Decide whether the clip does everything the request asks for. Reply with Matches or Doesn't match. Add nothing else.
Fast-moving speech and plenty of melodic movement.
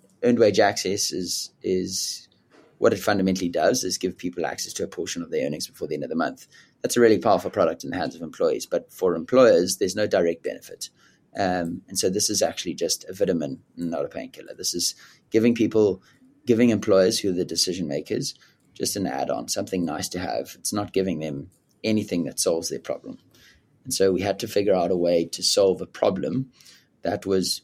Matches